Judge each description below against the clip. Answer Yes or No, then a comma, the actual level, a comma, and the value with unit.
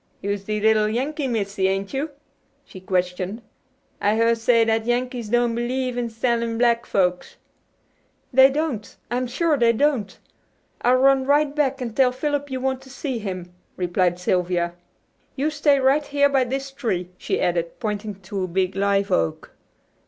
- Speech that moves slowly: No, average, 165 wpm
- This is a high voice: Yes, high, 235 Hz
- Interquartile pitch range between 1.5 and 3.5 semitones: No, average, 5.1 semitones